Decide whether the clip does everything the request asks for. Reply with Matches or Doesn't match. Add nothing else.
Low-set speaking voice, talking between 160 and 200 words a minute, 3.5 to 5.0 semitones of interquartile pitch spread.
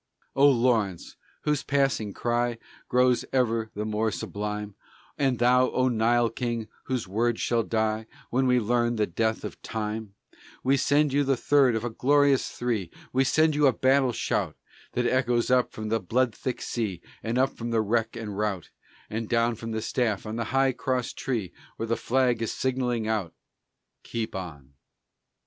Doesn't match